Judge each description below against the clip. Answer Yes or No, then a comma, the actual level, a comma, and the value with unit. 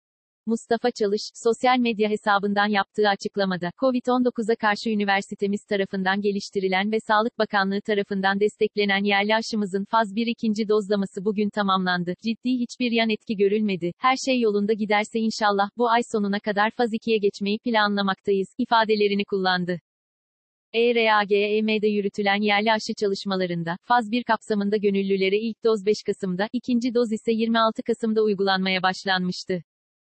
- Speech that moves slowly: No, average, 130 wpm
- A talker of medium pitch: No, high, 210 Hz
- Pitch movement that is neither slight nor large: No, narrow, 2.1 semitones